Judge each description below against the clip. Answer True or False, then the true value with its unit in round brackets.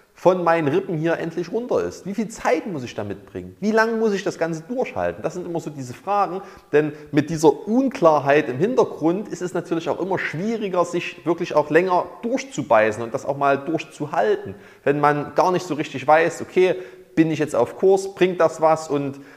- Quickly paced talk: True (205 wpm)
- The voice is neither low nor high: True (165 Hz)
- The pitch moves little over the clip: False (3.8 semitones)